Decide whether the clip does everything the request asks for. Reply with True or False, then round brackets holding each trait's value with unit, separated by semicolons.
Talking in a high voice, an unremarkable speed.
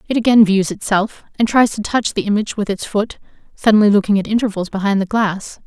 False (210 Hz; 210 wpm)